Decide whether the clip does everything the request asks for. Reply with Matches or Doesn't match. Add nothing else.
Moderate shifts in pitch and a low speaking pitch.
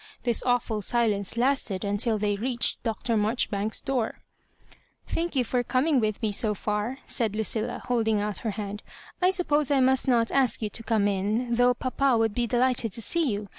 Doesn't match